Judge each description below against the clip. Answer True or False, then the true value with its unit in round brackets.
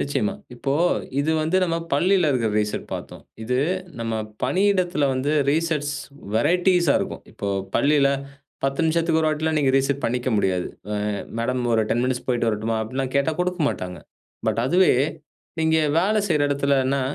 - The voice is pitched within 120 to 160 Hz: True (140 Hz)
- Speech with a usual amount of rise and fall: True (4.7 semitones)